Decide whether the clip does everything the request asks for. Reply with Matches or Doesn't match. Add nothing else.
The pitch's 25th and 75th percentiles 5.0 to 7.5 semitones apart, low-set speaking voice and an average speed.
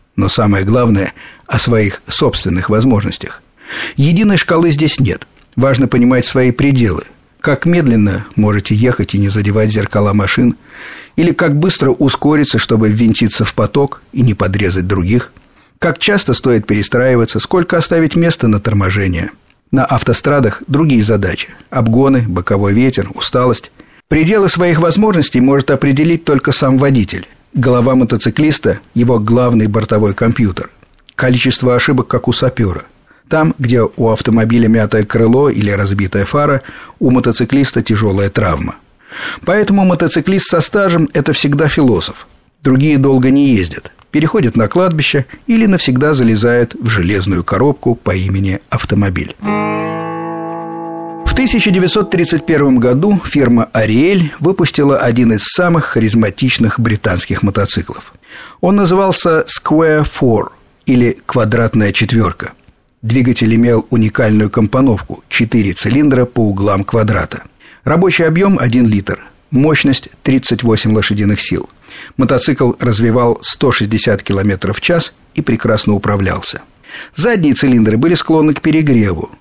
Matches